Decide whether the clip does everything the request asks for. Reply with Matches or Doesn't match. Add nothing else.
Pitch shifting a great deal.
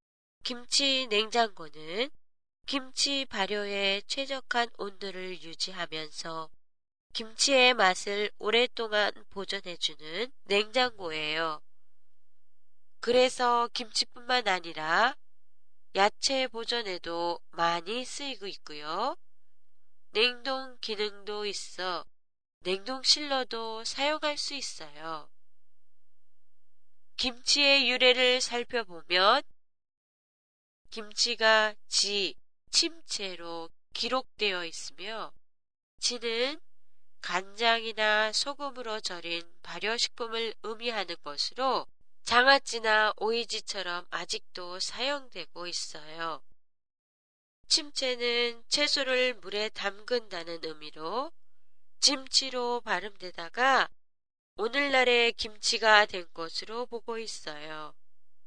Matches